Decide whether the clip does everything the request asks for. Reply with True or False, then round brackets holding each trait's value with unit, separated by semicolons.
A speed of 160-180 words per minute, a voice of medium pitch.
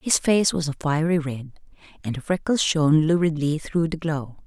False (190 wpm; 155 Hz)